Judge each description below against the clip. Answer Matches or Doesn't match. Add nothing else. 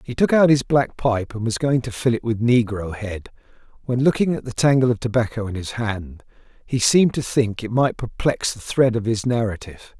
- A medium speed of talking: Doesn't match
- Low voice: Matches